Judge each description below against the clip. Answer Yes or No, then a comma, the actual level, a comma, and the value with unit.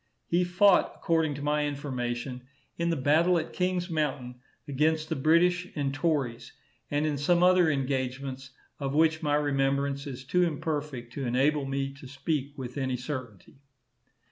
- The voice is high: No, medium, 145 Hz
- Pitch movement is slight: No, average, 3.2 semitones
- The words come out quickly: No, average, 155 wpm